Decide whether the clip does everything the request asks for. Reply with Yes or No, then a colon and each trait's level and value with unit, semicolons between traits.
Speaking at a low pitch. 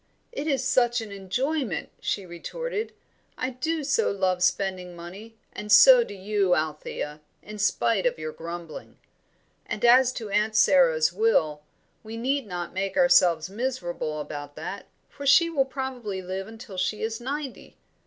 No: high, 210 Hz